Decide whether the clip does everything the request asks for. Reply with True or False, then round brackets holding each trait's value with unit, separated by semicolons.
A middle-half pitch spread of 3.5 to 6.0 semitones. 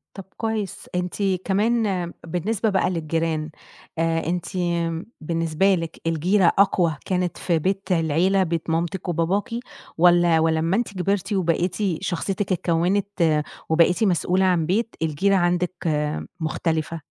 False (2.9 semitones)